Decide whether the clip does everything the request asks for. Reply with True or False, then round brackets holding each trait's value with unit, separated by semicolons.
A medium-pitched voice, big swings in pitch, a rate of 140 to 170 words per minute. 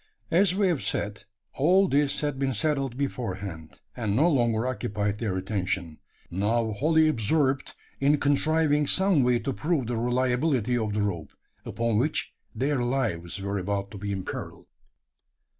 False (120 Hz; 6.0 semitones; 150 wpm)